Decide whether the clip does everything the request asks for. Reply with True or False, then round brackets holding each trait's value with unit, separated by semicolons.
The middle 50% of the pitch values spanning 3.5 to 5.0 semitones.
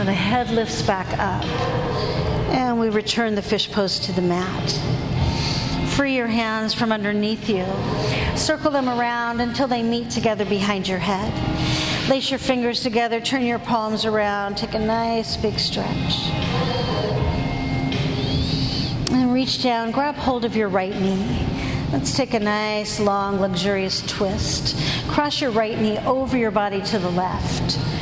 False (3.1 semitones)